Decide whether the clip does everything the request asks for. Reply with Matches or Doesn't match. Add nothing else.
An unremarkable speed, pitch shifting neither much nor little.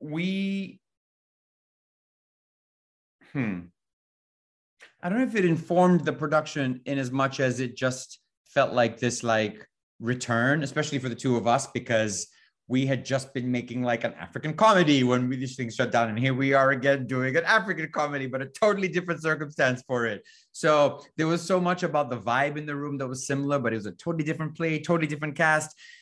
Matches